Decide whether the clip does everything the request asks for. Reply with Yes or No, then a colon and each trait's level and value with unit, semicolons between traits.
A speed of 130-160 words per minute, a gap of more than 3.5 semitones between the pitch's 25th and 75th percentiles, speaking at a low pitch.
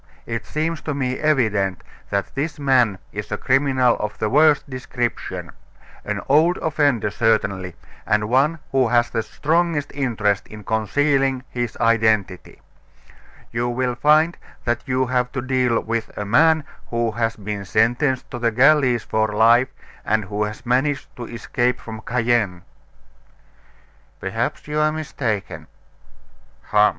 Yes: average, 140 wpm; average, 4.2 semitones; low, 120 Hz